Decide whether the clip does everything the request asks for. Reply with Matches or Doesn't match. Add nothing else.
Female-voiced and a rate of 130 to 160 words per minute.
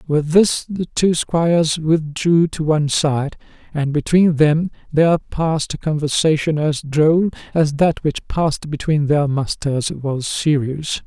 Doesn't match